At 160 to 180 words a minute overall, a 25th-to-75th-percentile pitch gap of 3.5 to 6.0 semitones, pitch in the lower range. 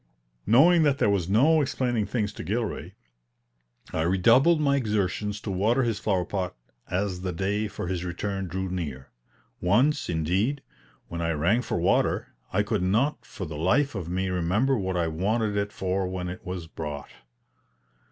Yes: average, 170 wpm; average, 4.3 semitones; very low, 95 Hz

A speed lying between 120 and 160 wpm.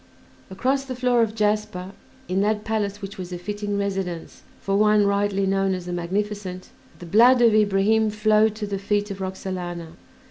No: average, 175 wpm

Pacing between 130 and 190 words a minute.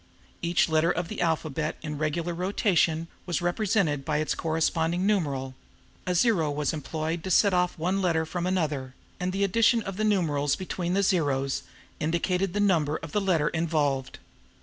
Yes: average, 170 wpm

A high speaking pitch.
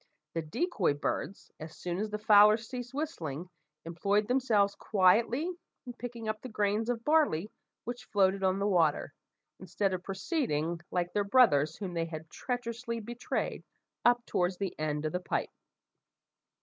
Yes: high, 205 Hz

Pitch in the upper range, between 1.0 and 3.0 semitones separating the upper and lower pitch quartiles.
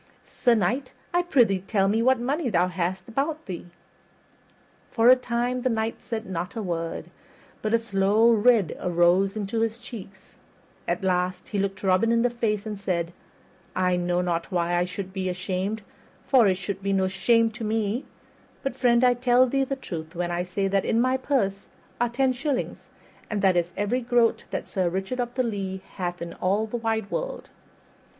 No: high, 210 Hz; average, 4.5 semitones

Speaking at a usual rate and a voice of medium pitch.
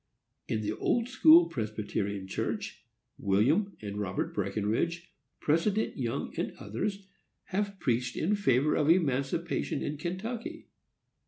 No: slow, 115 wpm; medium, 150 Hz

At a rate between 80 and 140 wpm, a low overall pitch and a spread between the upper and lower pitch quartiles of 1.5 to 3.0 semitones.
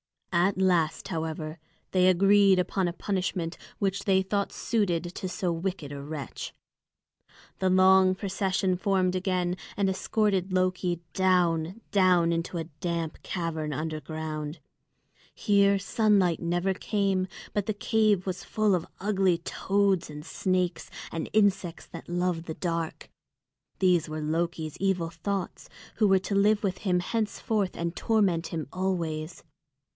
No: slow, 135 wpm; medium, 185 Hz; narrow, 2.6 semitones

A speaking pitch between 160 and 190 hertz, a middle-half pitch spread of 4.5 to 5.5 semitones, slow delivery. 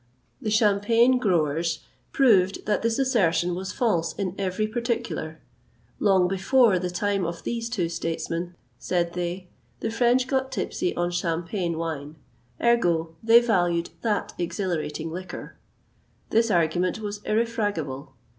Yes: medium, 185 Hz; average, 5.0 semitones; slow, 125 wpm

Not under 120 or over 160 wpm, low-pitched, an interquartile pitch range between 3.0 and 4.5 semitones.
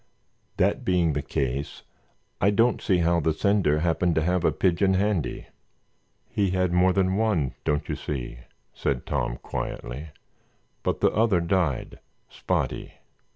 Yes: average, 140 wpm; very low, 85 Hz; average, 4.2 semitones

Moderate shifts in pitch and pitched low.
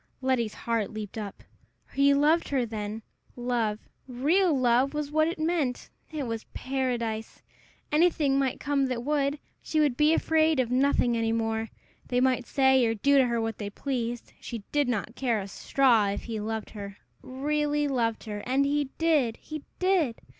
No: average, 4.2 semitones; very high, 255 Hz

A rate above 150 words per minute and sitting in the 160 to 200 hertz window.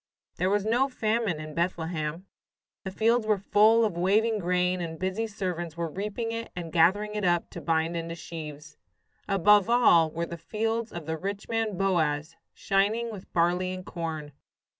Yes: average, 170 wpm; medium, 185 Hz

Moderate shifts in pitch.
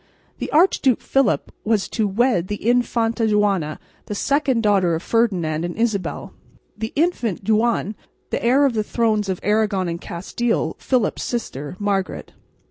Yes: average, 3.9 semitones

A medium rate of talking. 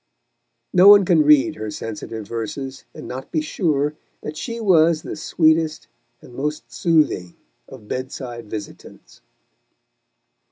No: slow, 130 wpm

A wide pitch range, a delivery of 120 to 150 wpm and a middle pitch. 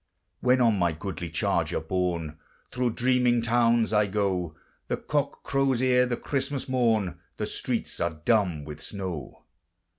No: wide, 6.1 semitones; average, 145 wpm; low, 110 Hz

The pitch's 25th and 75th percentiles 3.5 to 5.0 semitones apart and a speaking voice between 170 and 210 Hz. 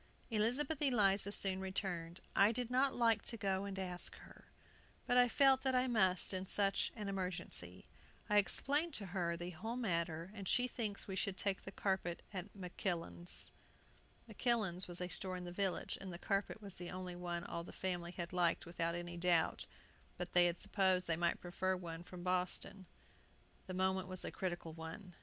No: average, 2.7 semitones; high, 190 Hz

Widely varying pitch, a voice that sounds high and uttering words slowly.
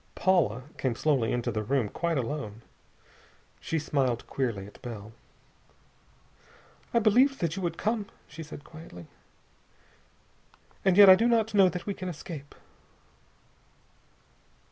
No: wide, 7.7 semitones; medium, 155 Hz; slow, 130 wpm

